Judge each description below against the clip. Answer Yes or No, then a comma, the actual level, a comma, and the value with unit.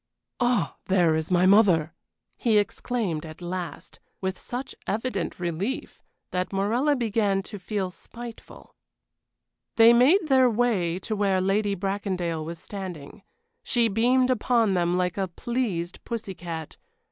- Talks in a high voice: Yes, high, 195 Hz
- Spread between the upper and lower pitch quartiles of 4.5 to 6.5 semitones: Yes, average, 4.8 semitones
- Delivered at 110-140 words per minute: Yes, slow, 135 wpm